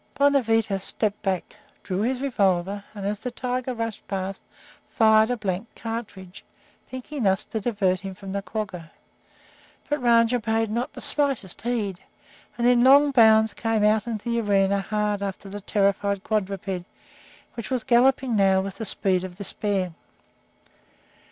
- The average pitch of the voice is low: No, high, 210 Hz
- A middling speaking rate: Yes, average, 150 wpm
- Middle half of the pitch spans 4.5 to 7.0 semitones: No, average, 3.4 semitones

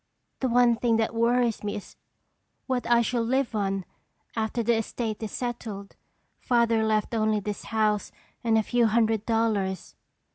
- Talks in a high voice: Yes, high, 225 Hz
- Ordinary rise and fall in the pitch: No, narrow, 1.8 semitones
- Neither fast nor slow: Yes, average, 155 wpm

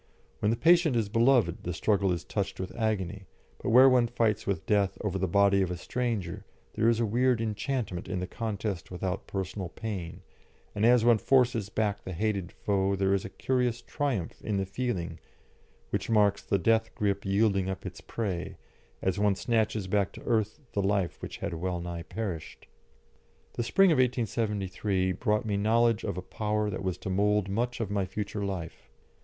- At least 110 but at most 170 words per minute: No, average, 185 wpm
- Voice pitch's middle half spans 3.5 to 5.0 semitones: No, average, 3.1 semitones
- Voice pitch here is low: Yes, low, 105 Hz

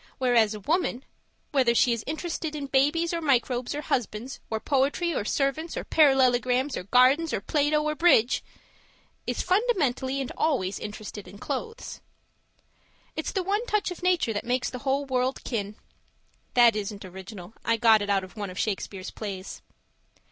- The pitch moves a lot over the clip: Yes, wide, 5.9 semitones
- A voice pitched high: Yes, very high, 255 Hz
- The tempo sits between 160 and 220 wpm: Yes, average, 165 wpm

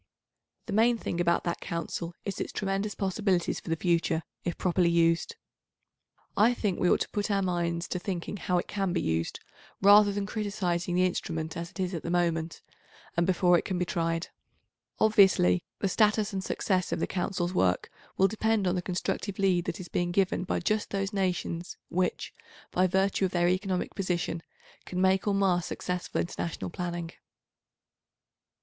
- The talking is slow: No, average, 180 wpm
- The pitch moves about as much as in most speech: No, narrow, 2.3 semitones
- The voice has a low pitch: No, medium, 180 Hz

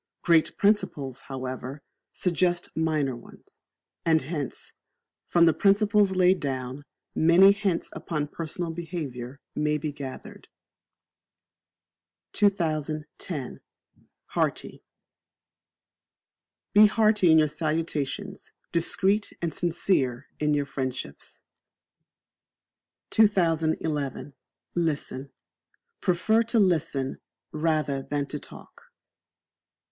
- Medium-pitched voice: Yes, medium, 160 Hz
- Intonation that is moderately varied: Yes, average, 4.1 semitones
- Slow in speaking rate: Yes, slow, 85 wpm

